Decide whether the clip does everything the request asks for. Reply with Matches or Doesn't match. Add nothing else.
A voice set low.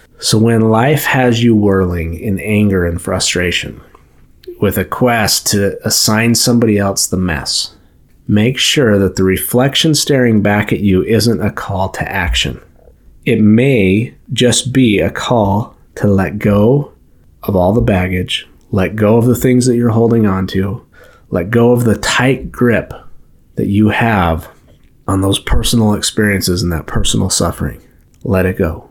Matches